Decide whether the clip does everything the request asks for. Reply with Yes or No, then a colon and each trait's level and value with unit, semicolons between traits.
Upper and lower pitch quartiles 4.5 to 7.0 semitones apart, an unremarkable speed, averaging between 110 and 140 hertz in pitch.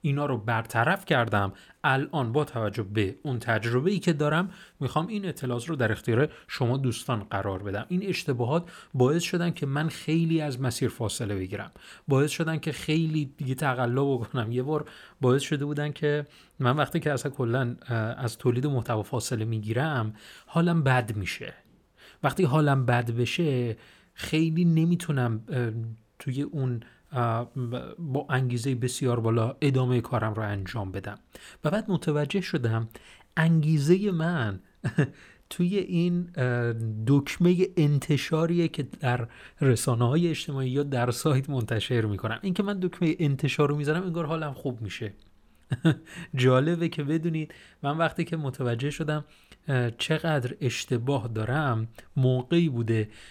Yes: average, 4.9 semitones; average, 135 wpm; low, 135 Hz